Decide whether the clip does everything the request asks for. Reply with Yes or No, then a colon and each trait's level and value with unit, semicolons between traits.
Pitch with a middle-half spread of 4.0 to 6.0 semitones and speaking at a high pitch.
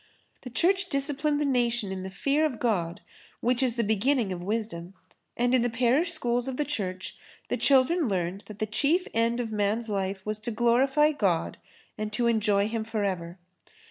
Yes: average, 4.7 semitones; high, 230 Hz